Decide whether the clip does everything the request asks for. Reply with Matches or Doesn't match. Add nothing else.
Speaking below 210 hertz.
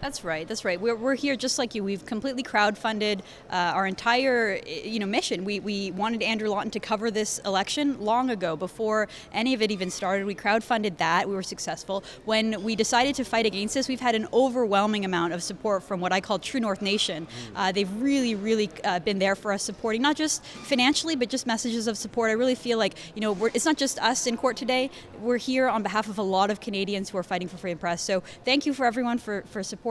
Doesn't match